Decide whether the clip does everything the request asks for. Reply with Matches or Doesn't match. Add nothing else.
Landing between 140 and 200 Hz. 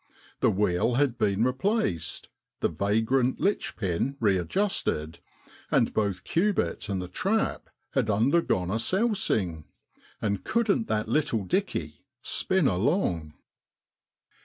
Doesn't match